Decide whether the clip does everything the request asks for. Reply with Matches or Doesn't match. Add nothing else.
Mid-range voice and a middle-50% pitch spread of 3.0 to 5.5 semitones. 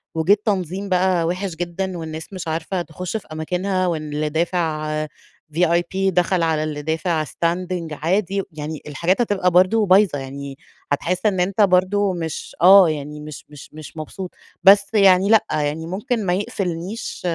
Matches